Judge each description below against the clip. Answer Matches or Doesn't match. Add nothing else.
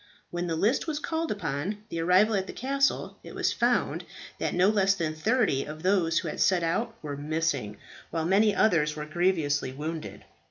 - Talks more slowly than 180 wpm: Doesn't match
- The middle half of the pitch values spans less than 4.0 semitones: Doesn't match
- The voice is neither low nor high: Matches